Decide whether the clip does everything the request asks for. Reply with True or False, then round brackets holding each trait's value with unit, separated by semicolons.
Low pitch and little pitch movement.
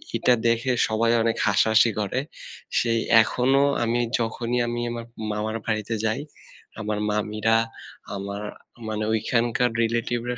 True (115 Hz; 1.7 semitones)